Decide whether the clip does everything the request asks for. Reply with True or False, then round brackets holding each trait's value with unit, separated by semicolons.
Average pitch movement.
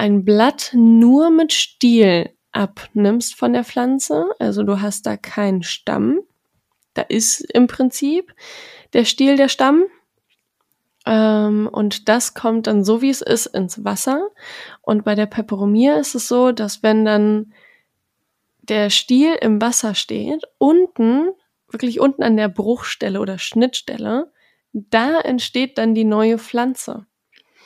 True (4.5 semitones)